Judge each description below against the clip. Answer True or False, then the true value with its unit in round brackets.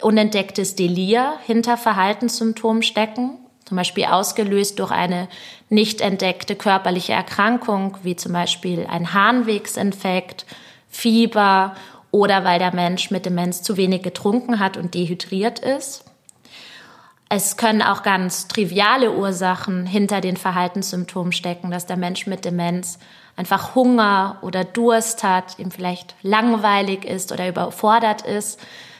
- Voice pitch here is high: True (195 Hz)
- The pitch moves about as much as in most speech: True (3.3 semitones)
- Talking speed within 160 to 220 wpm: False (125 wpm)